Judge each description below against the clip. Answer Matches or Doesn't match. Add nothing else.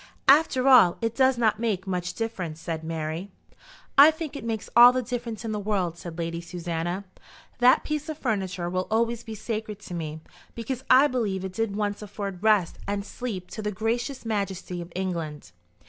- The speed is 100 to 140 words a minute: Doesn't match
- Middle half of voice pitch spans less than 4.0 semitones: Doesn't match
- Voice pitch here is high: Matches